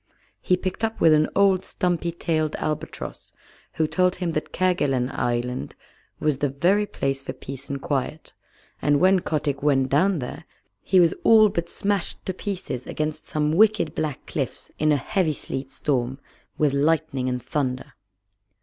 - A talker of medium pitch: Yes, medium, 155 Hz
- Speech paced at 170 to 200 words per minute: No, average, 160 wpm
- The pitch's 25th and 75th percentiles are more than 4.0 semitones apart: Yes, average, 4.9 semitones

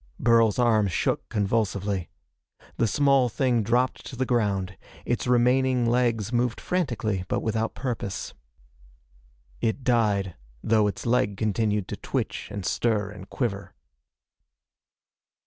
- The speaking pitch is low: Yes, low, 115 Hz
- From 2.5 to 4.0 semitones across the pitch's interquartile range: Yes, average, 3.2 semitones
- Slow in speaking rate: Yes, slow, 120 wpm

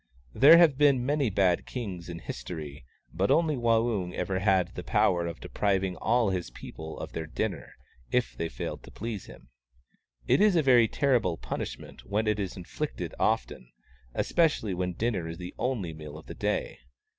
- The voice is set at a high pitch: No, low, 100 Hz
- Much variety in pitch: Yes, wide, 6.0 semitones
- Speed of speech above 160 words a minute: Yes, average, 175 wpm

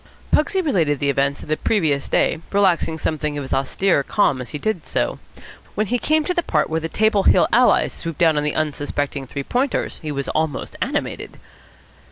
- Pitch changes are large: Yes, wide, 6.2 semitones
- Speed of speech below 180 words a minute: No, average, 200 wpm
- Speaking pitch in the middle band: Yes, medium, 160 Hz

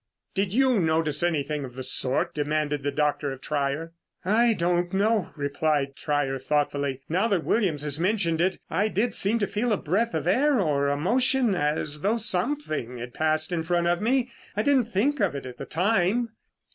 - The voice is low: No, medium, 170 Hz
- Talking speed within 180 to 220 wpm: Yes, average, 190 wpm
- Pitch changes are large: Yes, wide, 6.6 semitones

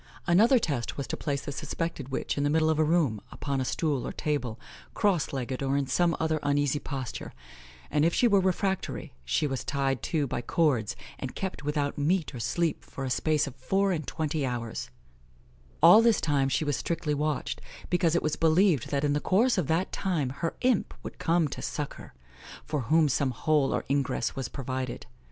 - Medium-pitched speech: Yes, medium, 150 Hz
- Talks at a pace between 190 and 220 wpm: Yes, average, 200 wpm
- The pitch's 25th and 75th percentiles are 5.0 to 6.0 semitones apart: No, average, 3.7 semitones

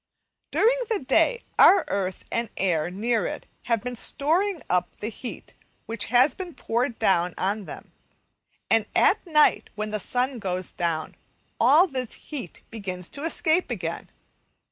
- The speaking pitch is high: Yes, high, 230 Hz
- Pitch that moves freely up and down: Yes, wide, 7.1 semitones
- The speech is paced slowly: No, average, 155 wpm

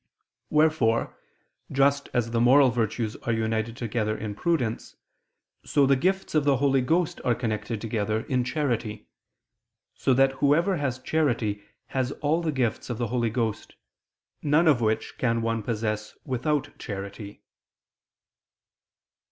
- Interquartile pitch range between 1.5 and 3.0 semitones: No, average, 4.2 semitones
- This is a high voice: No, low, 120 Hz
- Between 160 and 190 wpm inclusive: No, slow, 135 wpm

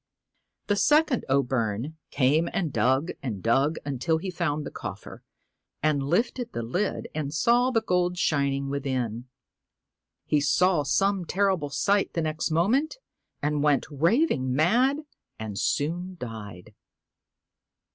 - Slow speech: Yes, slow, 130 wpm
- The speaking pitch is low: No, medium, 155 Hz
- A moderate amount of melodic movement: No, wide, 5.9 semitones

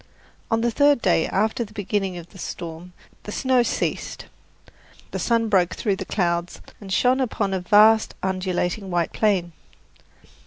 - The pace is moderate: Yes, average, 155 wpm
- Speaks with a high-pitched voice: Yes, high, 200 Hz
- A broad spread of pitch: No, average, 3.8 semitones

